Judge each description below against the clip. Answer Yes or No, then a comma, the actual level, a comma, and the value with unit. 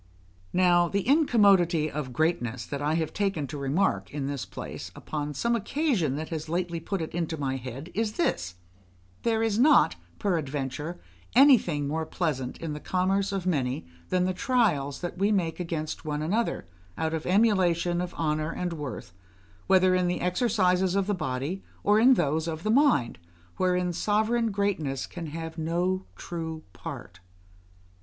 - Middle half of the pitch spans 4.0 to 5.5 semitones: Yes, average, 4.5 semitones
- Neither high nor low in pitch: Yes, medium, 175 Hz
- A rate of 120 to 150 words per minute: No, average, 165 wpm